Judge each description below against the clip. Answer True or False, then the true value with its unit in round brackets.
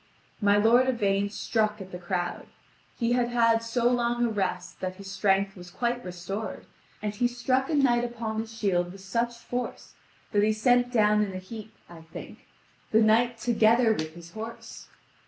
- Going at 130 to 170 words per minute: False (180 wpm)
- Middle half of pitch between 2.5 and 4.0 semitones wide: True (3.5 semitones)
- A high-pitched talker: True (220 Hz)